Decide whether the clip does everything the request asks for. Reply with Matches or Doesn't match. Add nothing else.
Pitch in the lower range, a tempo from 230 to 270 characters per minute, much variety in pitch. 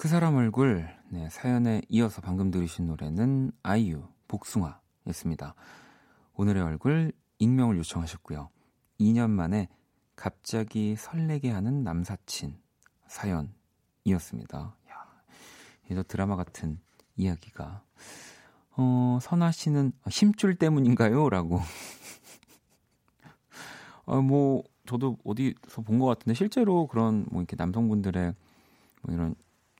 Matches